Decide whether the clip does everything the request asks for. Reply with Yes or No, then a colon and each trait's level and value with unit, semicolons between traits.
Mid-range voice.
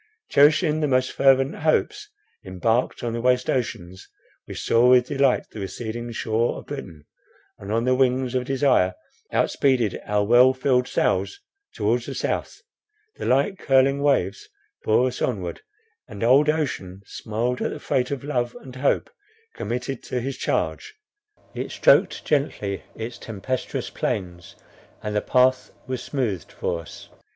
No: low, 125 Hz